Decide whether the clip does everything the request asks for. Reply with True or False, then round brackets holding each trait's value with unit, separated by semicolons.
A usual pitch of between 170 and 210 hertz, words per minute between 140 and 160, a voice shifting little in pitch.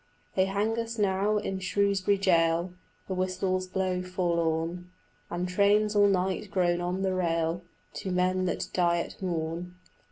True (185 Hz; 150 wpm; 1.9 semitones)